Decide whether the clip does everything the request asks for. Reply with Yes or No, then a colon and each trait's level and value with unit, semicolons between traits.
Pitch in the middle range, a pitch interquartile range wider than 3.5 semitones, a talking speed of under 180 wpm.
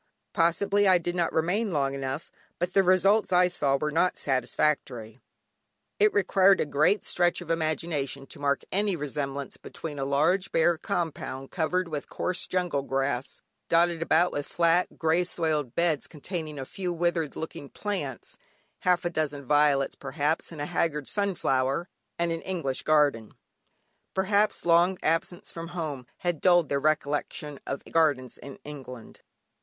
Yes: medium, 160 Hz; average, 3.9 semitones; average, 150 wpm